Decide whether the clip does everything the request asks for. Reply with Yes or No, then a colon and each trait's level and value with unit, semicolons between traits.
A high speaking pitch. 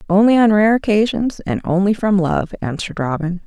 Yes: high, 195 Hz